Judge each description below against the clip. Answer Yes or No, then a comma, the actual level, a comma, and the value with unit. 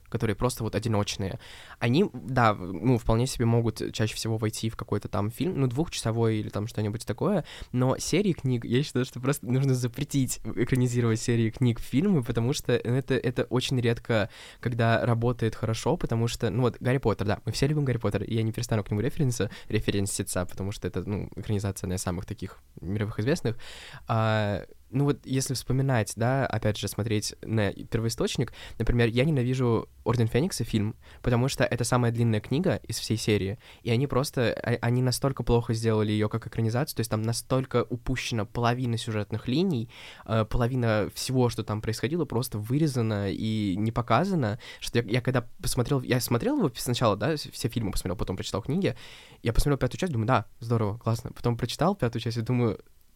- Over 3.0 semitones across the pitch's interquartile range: No, average, 2.7 semitones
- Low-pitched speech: Yes, low, 115 Hz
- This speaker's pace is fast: Yes, fast, 180 wpm